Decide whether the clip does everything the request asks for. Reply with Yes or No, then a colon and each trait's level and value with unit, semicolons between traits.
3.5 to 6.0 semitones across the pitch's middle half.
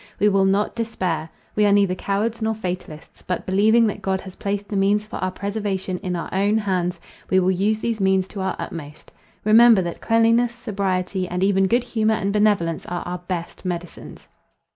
No: average, 2.7 semitones